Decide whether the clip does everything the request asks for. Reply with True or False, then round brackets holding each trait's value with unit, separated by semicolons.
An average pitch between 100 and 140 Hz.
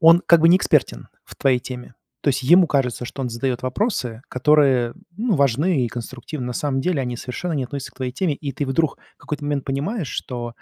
True (135 Hz)